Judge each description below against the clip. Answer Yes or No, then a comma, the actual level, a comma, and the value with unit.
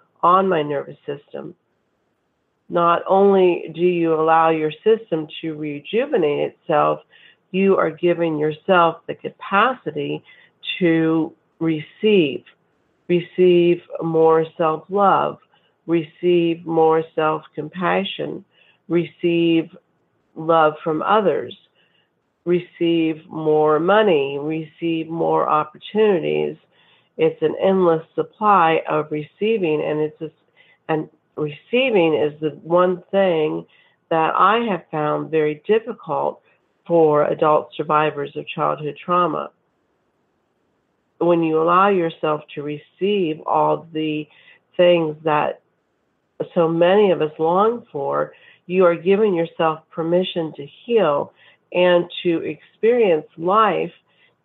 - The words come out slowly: Yes, slow, 100 wpm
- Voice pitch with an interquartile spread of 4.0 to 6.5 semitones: No, narrow, 2.5 semitones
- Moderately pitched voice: Yes, medium, 165 Hz